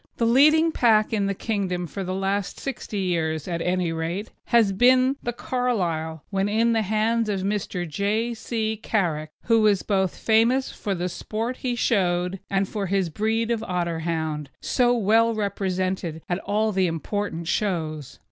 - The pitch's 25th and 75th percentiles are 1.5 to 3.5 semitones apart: No, average, 4.2 semitones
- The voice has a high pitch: Yes, high, 200 Hz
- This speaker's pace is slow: No, average, 165 wpm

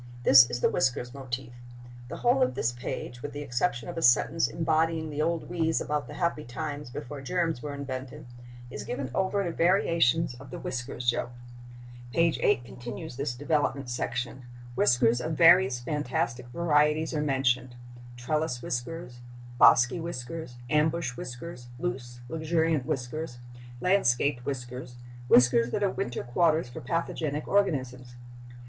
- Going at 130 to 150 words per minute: Yes, average, 140 wpm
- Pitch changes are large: No, average, 4.8 semitones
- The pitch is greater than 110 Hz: Yes, low, 135 Hz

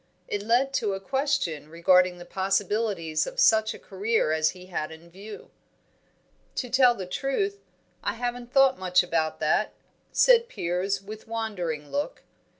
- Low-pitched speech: No, high, 205 Hz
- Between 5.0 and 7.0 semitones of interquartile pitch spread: Yes, wide, 5.6 semitones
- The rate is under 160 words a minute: Yes, average, 150 wpm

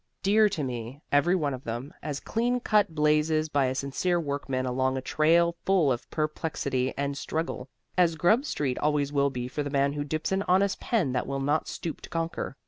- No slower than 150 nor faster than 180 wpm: No, fast, 205 wpm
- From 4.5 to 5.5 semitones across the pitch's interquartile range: No, average, 3.8 semitones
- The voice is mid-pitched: Yes, medium, 150 Hz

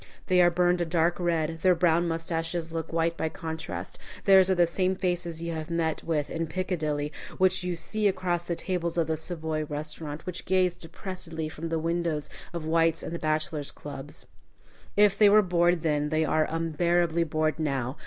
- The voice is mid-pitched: Yes, medium, 165 Hz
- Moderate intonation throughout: No, narrow, 1.9 semitones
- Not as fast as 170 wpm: No, average, 185 wpm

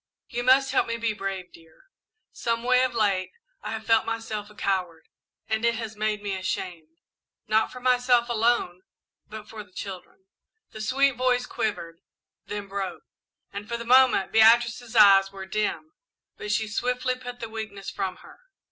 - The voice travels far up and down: No, average, 3.5 semitones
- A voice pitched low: No, high, 220 Hz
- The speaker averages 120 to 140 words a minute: No, average, 170 wpm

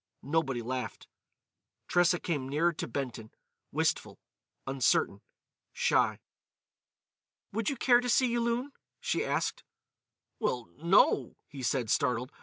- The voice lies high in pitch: No, medium, 150 Hz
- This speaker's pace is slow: Yes, slow, 105 wpm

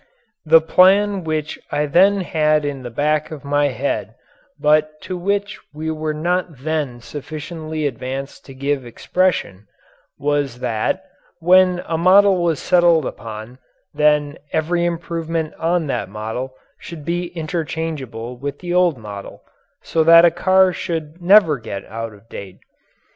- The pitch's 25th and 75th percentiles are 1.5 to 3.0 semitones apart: No, average, 4.2 semitones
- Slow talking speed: No, average, 145 wpm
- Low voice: No, medium, 155 Hz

